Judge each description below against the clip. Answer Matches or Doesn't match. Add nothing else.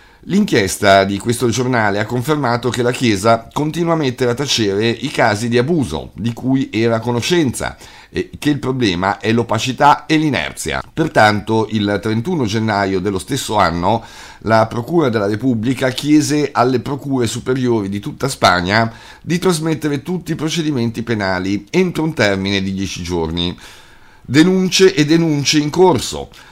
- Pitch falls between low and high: Doesn't match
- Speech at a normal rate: Matches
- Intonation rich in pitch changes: Matches